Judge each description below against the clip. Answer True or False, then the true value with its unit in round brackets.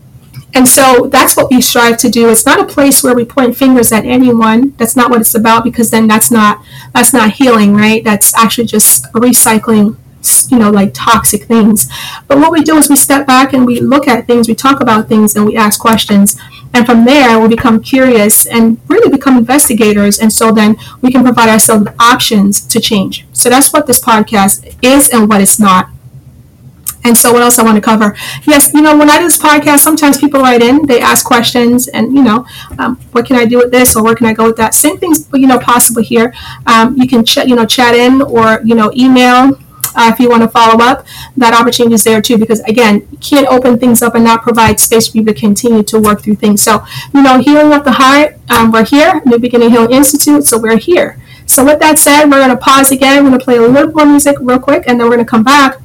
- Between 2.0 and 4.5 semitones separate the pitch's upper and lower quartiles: True (3.1 semitones)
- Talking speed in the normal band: False (240 wpm)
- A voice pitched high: True (240 Hz)